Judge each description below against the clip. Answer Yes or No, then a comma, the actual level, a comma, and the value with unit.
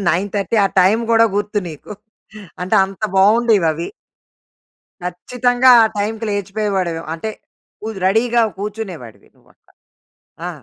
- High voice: Yes, high, 205 Hz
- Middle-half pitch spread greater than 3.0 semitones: Yes, average, 3.4 semitones